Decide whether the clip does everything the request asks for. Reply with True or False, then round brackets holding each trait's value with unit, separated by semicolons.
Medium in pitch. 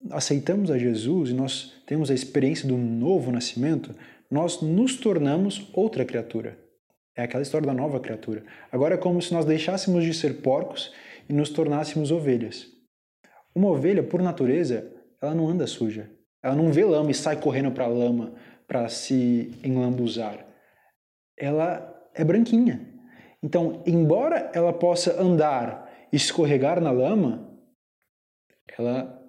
True (150 Hz)